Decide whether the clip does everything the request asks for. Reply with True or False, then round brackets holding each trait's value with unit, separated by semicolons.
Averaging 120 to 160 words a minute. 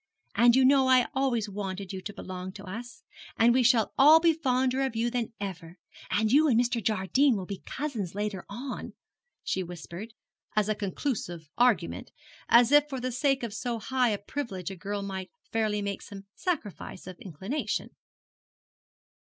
False (175 wpm)